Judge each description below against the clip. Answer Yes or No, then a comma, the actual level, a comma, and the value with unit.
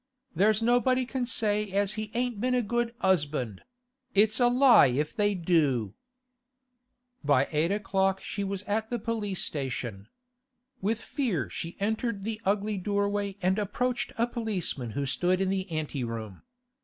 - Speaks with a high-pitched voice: Yes, high, 200 Hz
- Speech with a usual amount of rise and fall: No, wide, 5.8 semitones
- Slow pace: No, average, 155 wpm